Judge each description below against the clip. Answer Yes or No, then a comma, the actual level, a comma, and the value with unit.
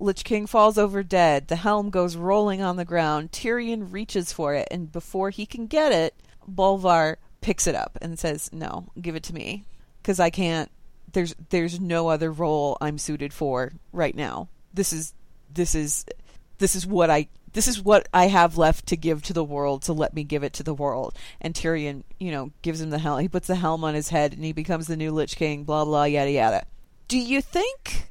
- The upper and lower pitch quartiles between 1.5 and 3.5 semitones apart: No, average, 4.0 semitones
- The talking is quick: Yes, fast, 220 wpm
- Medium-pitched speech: Yes, medium, 165 Hz